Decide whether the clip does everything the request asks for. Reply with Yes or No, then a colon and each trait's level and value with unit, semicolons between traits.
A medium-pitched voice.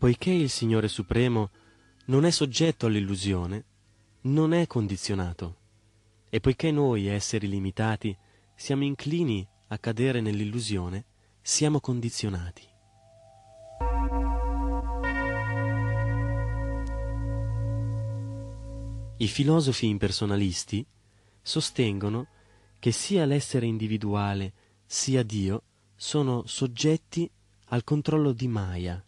No: low, 110 Hz